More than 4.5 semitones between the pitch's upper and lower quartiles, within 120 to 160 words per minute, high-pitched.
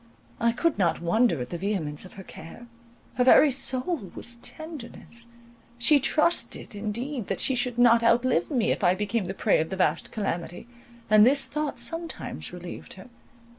No: wide, 5.4 semitones; average, 170 wpm; high, 235 Hz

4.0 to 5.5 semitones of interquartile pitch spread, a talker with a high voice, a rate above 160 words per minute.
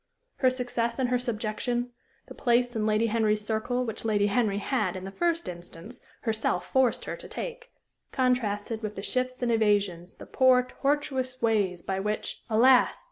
No: average, 3.2 semitones; high, 230 Hz; average, 170 wpm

